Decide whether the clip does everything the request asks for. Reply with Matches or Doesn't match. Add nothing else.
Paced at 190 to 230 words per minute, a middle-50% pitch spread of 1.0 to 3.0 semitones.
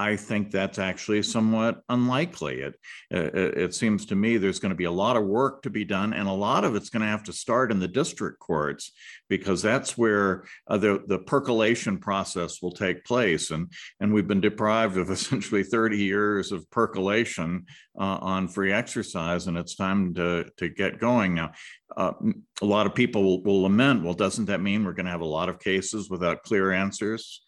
Matches